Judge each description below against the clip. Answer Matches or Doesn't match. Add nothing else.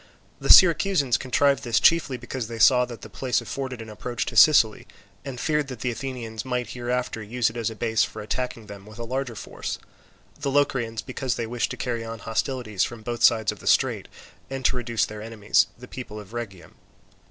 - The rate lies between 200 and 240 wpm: Matches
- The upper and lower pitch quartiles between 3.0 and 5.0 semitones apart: Doesn't match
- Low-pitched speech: Matches